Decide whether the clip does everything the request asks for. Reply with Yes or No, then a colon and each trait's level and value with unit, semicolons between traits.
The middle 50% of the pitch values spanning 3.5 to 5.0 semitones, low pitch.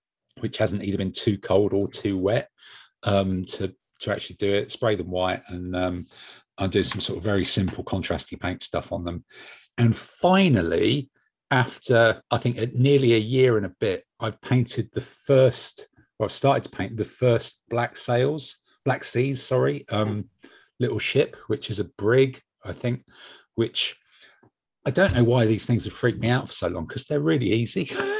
Yes: average, 4.4 semitones; low, 115 Hz